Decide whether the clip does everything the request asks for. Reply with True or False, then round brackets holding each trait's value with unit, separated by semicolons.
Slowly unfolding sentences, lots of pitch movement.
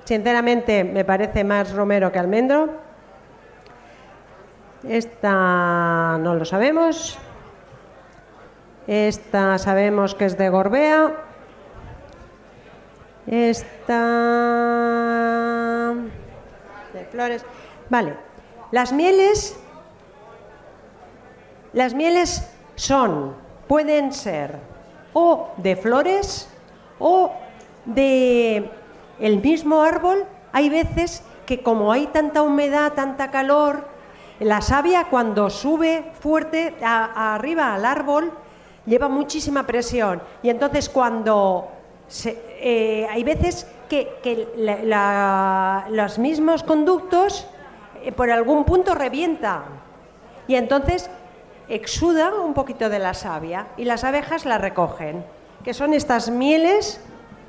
True (100 wpm; 6.1 semitones)